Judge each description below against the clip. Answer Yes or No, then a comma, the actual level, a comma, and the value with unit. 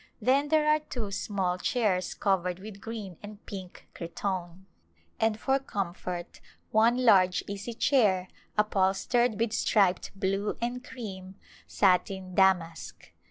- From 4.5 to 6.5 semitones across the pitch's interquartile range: No, average, 3.6 semitones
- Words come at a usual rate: No, slow, 120 wpm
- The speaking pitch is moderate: No, high, 200 Hz